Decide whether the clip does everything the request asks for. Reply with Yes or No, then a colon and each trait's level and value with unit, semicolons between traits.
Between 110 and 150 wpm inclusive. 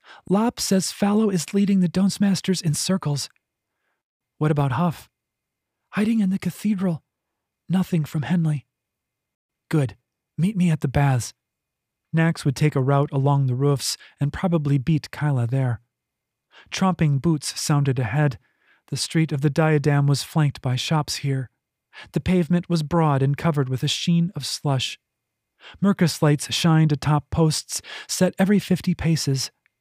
Yes: average, 145 wpm